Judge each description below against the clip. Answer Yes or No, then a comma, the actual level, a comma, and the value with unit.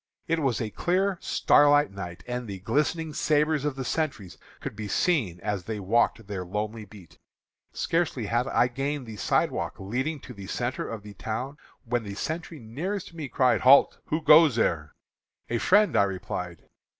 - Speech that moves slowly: No, average, 175 wpm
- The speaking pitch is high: No, low, 120 Hz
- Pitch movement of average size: No, wide, 6.5 semitones